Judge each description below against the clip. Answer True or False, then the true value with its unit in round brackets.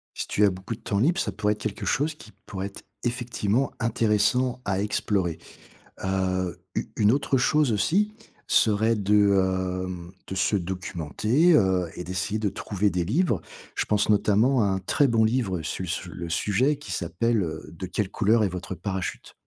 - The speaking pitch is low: True (105 Hz)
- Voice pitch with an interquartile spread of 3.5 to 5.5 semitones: True (4.0 semitones)